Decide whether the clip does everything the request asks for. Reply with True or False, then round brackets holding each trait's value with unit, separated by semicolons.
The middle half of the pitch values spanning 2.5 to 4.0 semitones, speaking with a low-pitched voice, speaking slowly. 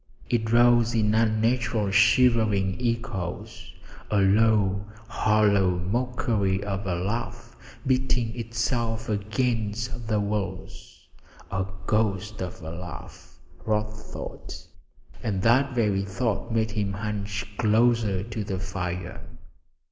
True (3.0 semitones; 105 Hz; 110 wpm)